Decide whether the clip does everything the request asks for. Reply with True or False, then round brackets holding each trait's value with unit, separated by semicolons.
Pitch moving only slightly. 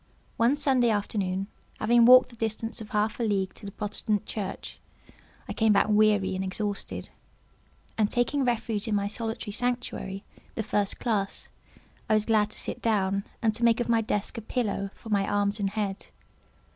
True (2.3 semitones)